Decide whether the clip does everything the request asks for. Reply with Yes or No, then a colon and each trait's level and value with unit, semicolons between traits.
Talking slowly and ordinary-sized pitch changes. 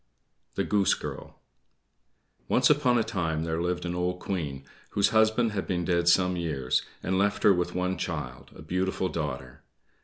No: average, 165 wpm; average, 3.4 semitones